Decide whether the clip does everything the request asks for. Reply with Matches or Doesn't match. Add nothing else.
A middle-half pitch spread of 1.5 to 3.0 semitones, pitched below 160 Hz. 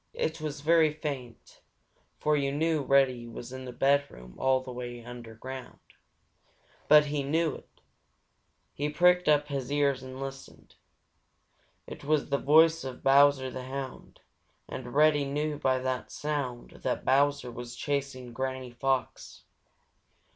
Matches